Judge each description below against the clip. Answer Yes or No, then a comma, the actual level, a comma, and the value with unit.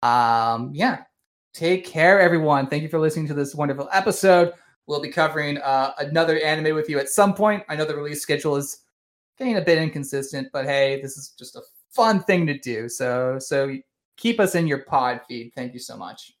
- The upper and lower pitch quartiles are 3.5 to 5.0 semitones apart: Yes, average, 3.9 semitones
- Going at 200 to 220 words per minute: Yes, fast, 205 wpm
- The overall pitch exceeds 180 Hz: No, medium, 145 Hz